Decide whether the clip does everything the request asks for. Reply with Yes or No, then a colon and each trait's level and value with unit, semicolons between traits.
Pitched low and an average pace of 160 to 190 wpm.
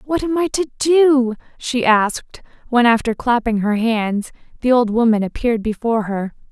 No: high, 240 Hz; average, 165 wpm